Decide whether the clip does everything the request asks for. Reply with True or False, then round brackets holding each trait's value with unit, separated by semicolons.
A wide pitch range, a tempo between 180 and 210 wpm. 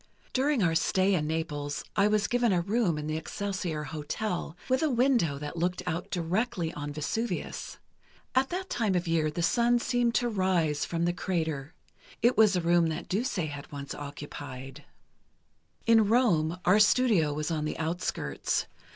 False (6.1 semitones; 170 wpm)